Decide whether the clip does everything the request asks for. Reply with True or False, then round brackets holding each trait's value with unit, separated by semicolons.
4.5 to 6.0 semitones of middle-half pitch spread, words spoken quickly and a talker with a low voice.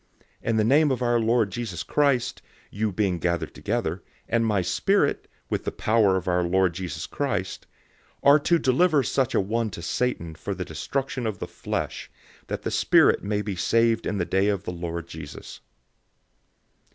False (4.9 semitones; 185 wpm; 105 Hz)